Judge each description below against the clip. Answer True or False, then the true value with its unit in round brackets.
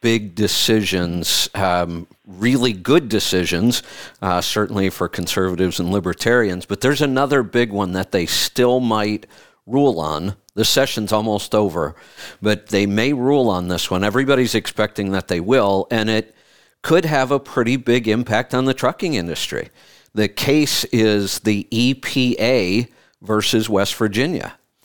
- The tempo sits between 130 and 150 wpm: True (145 wpm)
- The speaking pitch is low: True (110 Hz)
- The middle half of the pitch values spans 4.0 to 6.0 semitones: True (4.3 semitones)